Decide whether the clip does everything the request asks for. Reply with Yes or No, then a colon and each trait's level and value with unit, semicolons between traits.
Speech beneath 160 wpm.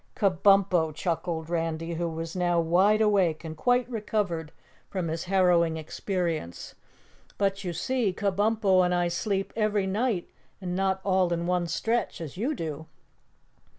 Yes: average, 145 wpm